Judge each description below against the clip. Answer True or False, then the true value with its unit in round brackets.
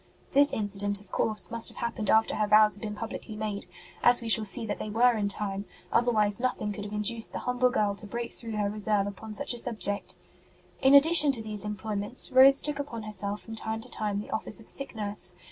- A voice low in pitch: False (215 Hz)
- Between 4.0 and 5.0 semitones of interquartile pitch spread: False (2.4 semitones)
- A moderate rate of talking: False (225 wpm)